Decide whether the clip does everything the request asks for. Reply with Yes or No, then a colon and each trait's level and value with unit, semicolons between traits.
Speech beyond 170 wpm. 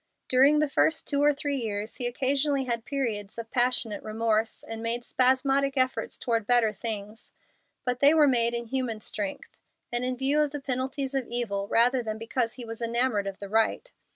Yes: average, 190 wpm